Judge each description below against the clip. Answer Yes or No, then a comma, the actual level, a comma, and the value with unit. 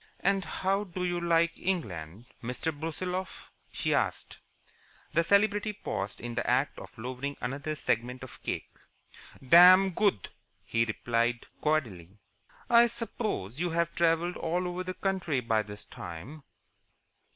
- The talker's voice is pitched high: No, medium, 165 Hz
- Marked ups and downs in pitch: Yes, wide, 7.5 semitones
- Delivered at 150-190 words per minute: No, slow, 135 wpm